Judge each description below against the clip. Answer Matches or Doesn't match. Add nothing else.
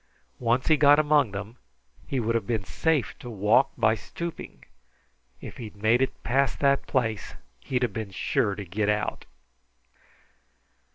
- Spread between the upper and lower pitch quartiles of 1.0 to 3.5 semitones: Doesn't match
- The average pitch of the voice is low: Matches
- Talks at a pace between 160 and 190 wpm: Doesn't match